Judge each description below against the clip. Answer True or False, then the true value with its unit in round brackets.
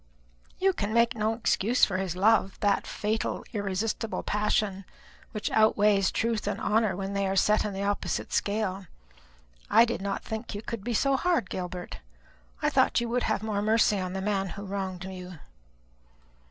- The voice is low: False (205 Hz)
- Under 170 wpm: False (175 wpm)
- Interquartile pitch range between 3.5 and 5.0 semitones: False (2.4 semitones)